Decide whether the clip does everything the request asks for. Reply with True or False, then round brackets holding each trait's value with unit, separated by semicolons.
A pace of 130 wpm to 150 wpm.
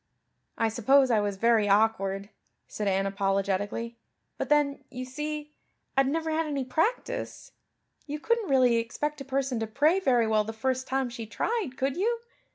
False (165 wpm)